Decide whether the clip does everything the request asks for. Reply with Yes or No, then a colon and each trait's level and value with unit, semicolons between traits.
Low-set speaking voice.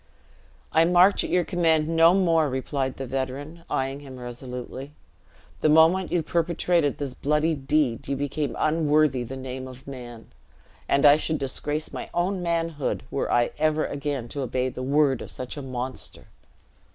No: medium, 145 Hz